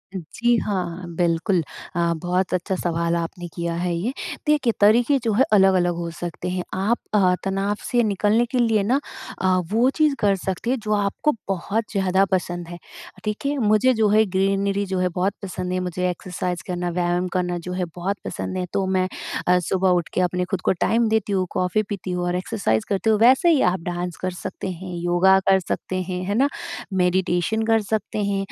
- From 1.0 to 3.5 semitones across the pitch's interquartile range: Yes, average, 3.0 semitones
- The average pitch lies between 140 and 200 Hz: Yes, high, 190 Hz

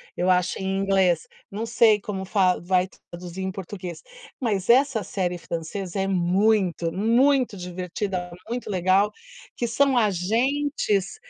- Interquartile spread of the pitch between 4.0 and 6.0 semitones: No, average, 3.5 semitones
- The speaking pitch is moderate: No, high, 195 Hz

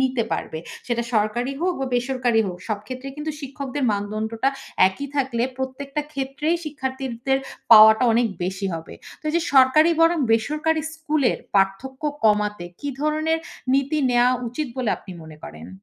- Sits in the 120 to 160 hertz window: No, very high, 260 Hz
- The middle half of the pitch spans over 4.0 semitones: Yes, average, 4.7 semitones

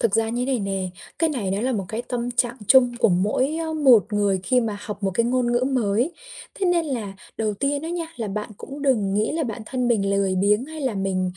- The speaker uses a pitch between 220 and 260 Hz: Yes, high, 235 Hz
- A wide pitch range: No, average, 4.7 semitones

